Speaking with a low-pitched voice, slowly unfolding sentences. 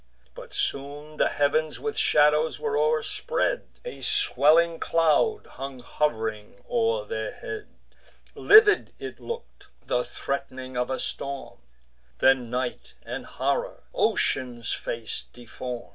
No: medium, 150 Hz; slow, 115 wpm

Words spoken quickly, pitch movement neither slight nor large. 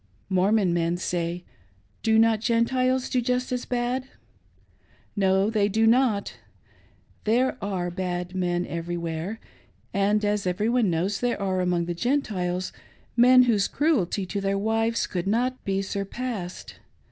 No: average, 140 wpm; average, 4.7 semitones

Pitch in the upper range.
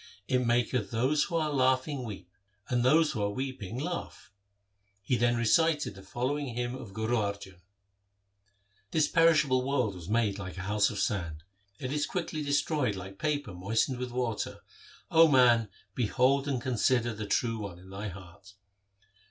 No: low, 120 Hz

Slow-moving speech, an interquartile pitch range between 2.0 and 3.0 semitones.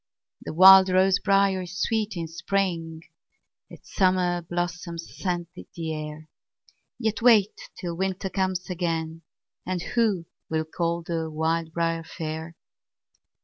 Yes: slow, 125 wpm; narrow, 2.6 semitones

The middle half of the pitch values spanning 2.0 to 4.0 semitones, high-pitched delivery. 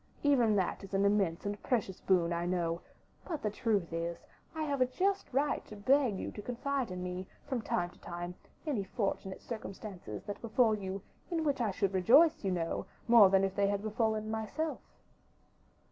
No: average, 4.9 semitones; high, 205 Hz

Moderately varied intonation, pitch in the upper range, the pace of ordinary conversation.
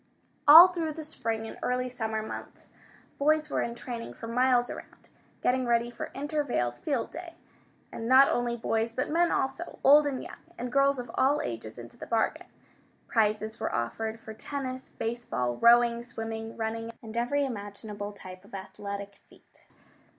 Yes: average, 3.5 semitones; high, 235 Hz; average, 165 wpm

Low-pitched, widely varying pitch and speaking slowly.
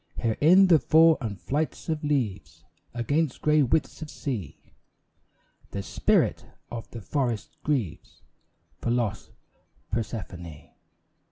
Yes: low, 120 Hz; wide, 7.0 semitones; slow, 115 wpm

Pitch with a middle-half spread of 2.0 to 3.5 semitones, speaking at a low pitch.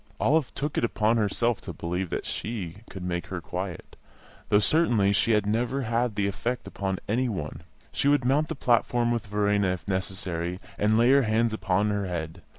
No: average, 4.1 semitones; low, 105 Hz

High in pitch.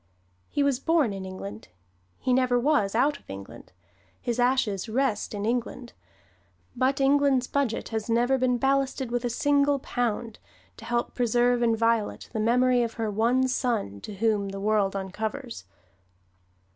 Yes: high, 240 Hz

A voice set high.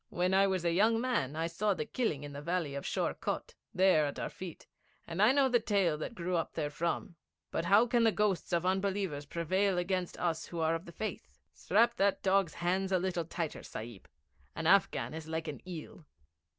No: medium, 180 Hz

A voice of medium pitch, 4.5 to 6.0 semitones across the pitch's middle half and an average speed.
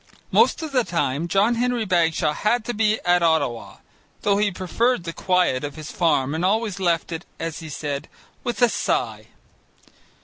Yes: medium, 180 Hz; wide, 5.4 semitones; average, 175 wpm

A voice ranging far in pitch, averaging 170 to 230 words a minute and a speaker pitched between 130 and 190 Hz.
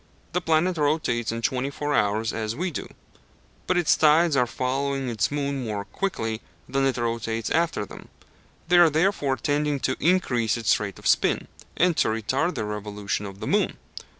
Yes: wide, 5.8 semitones; average, 180 wpm; low, 135 Hz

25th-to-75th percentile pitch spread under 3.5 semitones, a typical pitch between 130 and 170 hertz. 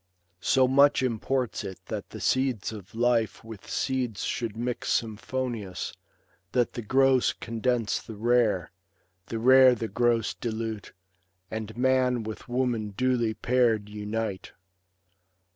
No: narrow, 2.6 semitones; low, 115 Hz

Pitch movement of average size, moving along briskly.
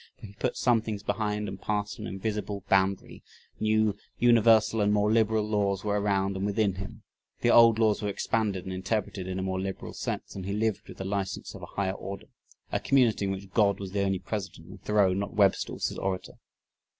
No: narrow, 1.9 semitones; fast, 210 wpm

